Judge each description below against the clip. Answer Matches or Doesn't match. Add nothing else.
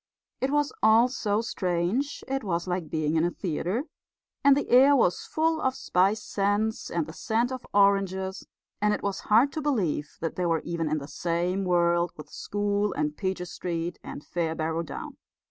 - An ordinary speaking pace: Matches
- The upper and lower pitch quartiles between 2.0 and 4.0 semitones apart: Doesn't match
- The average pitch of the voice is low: Doesn't match